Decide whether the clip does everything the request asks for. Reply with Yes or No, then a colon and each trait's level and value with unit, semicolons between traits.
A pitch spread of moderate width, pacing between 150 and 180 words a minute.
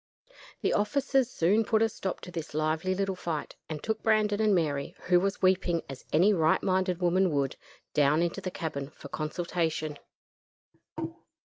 Yes: average, 4.0 semitones; average, 160 wpm